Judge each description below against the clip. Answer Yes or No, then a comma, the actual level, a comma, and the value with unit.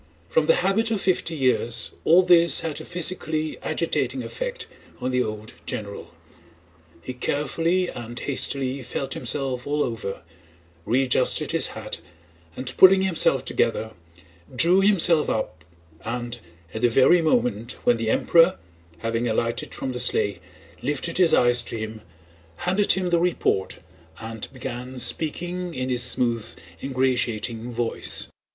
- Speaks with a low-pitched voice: Yes, low, 130 Hz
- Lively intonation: Yes, wide, 6.2 semitones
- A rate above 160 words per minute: No, slow, 135 wpm